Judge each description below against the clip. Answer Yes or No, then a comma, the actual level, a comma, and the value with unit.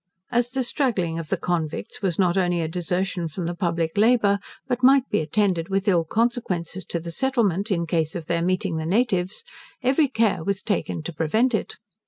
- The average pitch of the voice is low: No, medium, 185 Hz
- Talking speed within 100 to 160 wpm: No, average, 195 wpm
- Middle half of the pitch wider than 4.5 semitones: Yes, average, 4.9 semitones